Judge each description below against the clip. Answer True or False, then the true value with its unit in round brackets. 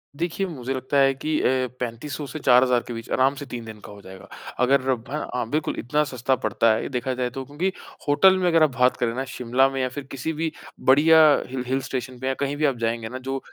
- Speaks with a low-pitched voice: True (130 Hz)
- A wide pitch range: False (2.8 semitones)